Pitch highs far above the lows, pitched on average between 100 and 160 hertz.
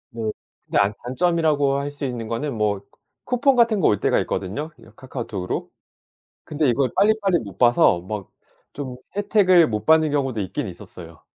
Yes: wide, 7.1 semitones; low, 135 Hz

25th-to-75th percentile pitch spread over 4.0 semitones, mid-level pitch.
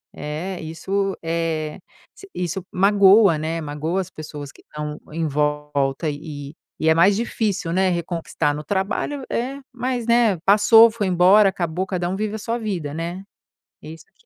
Yes: average, 4.6 semitones; medium, 175 Hz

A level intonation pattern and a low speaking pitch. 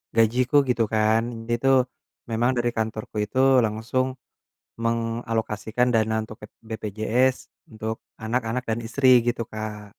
Yes: narrow, 1.7 semitones; low, 115 Hz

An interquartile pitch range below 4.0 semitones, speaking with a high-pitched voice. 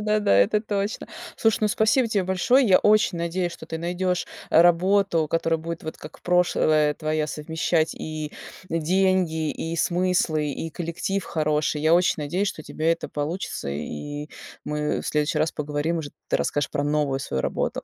No: average, 3.4 semitones; medium, 165 Hz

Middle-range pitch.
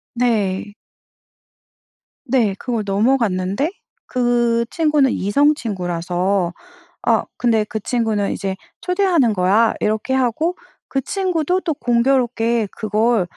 No: high, 235 Hz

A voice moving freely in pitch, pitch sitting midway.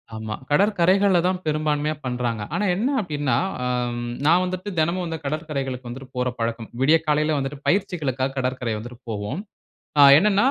Yes: wide, 5.7 semitones; medium, 145 Hz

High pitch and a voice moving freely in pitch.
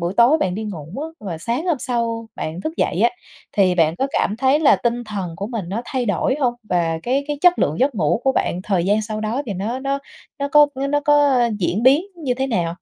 Yes: high, 235 Hz; wide, 6.2 semitones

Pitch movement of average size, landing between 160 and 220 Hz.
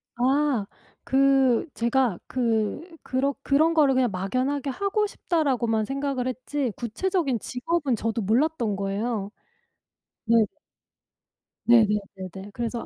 No: average, 3.8 semitones; very high, 255 Hz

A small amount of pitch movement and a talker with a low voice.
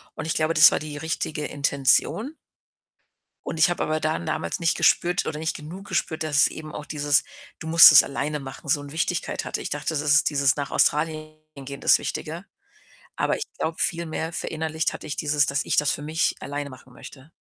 No: narrow, 1.9 semitones; medium, 155 Hz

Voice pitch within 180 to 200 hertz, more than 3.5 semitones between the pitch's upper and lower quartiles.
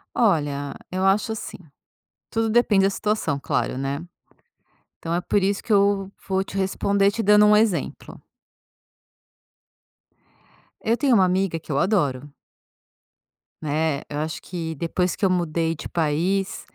Yes: medium, 185 Hz; average, 4.1 semitones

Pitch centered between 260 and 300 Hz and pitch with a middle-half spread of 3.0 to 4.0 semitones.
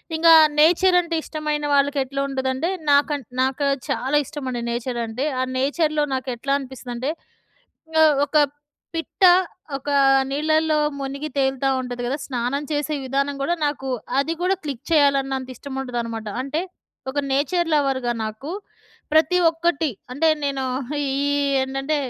No: very high, 275 Hz; narrow, 2.5 semitones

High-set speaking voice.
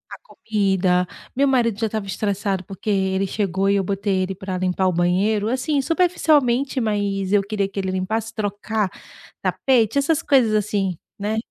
Yes: high, 205 Hz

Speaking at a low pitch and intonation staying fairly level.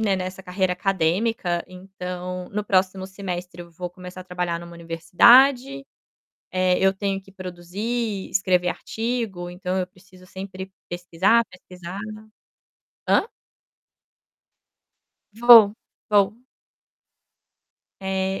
No: medium, 185 Hz; narrow, 1.8 semitones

